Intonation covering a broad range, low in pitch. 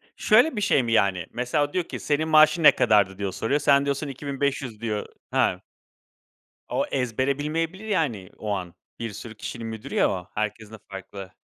Yes: wide, 5.8 semitones; low, 125 Hz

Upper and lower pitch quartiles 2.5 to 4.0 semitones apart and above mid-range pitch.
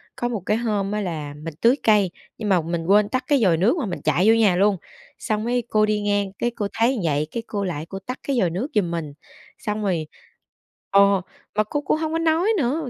No: average, 4.5 semitones; high, 210 Hz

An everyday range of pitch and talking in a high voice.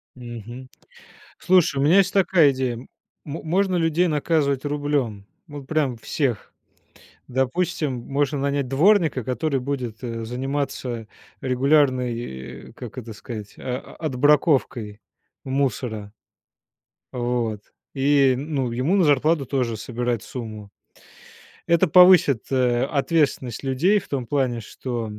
No: average, 3.6 semitones; low, 135 Hz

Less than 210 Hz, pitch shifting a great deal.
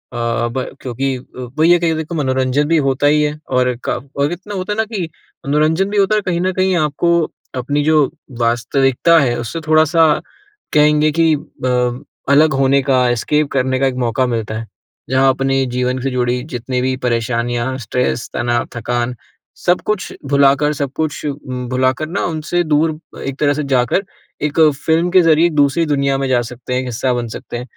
No: low, 135 Hz; average, 3.9 semitones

